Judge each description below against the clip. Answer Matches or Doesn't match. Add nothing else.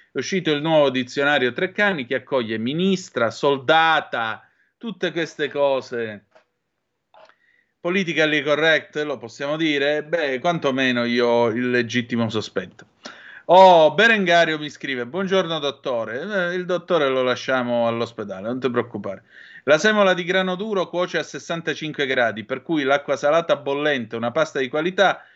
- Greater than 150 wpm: Doesn't match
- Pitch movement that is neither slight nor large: Doesn't match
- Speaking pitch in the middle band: Matches